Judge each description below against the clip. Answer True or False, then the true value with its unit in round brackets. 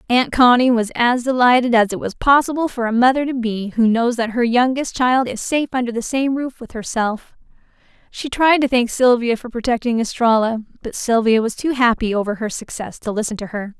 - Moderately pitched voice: False (240 Hz)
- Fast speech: True (210 wpm)